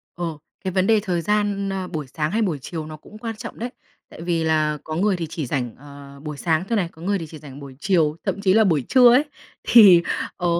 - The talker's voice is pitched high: No, medium, 170 Hz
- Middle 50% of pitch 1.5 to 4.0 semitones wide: No, average, 4.6 semitones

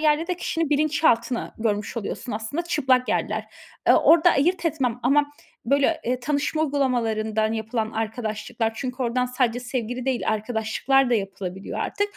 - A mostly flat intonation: No, average, 4.6 semitones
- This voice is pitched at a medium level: No, very high, 250 Hz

